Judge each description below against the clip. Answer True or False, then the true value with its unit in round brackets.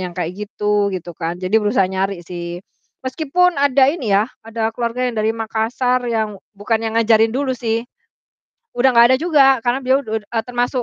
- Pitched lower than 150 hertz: False (225 Hz)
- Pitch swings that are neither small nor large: True (3.7 semitones)